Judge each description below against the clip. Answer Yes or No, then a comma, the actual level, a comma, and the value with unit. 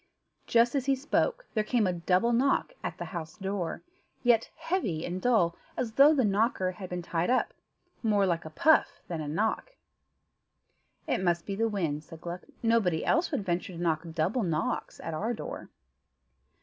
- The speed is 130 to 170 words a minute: No, average, 180 wpm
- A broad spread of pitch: Yes, wide, 5.8 semitones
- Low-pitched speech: No, high, 195 Hz